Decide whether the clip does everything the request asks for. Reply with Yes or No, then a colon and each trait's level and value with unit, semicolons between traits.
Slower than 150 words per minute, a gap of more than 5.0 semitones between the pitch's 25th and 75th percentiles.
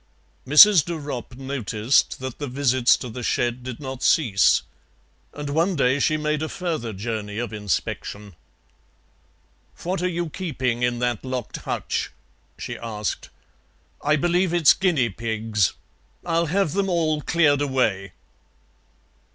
Yes: slow, 135 wpm; wide, 5.4 semitones